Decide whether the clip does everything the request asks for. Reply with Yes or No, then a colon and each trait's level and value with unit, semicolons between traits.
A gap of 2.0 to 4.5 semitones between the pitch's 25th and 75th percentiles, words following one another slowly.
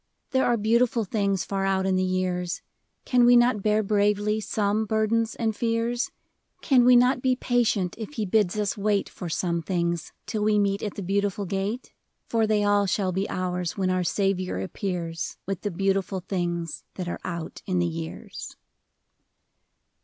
No: average, 2.9 semitones; average, 175 wpm